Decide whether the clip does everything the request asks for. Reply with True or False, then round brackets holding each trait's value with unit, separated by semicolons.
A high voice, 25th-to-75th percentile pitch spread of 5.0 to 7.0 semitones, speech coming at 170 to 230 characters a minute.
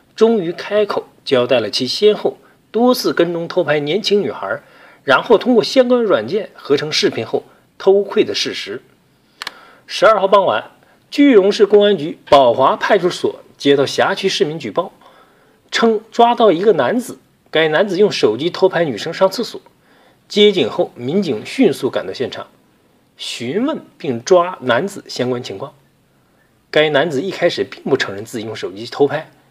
False (200 Hz; 5.3 semitones; 245 characters per minute)